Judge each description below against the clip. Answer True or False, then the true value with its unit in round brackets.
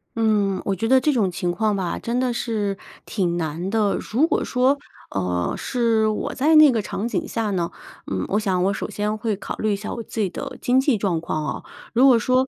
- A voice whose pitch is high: True (215 Hz)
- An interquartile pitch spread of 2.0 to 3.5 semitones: False (4.2 semitones)